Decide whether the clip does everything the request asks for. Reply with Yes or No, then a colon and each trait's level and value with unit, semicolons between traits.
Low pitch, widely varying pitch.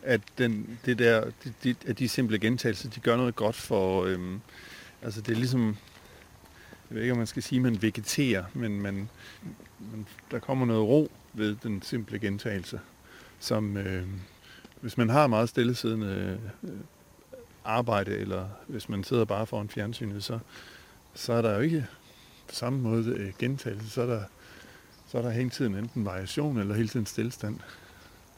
No: low, 110 Hz; average, 3.0 semitones